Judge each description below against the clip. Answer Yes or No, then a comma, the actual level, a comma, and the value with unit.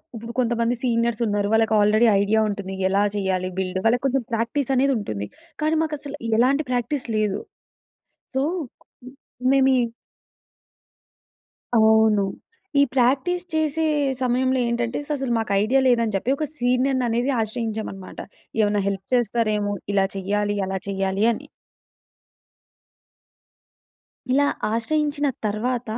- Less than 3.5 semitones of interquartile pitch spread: No, average, 4.1 semitones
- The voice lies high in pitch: Yes, high, 230 Hz